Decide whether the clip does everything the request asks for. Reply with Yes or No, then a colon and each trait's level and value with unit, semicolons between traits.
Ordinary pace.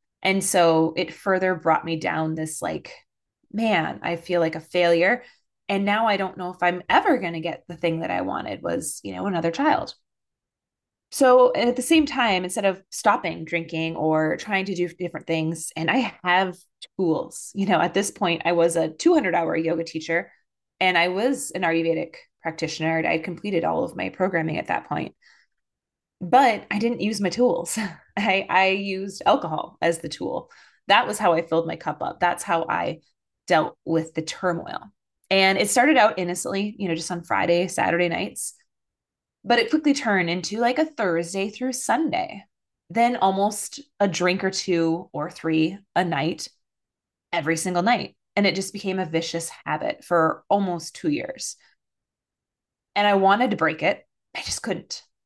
Yes: average, 180 wpm